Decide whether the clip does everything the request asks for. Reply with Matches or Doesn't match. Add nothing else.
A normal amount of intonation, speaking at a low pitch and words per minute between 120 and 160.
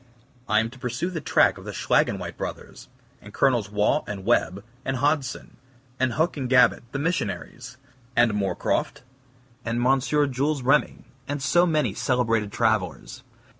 Matches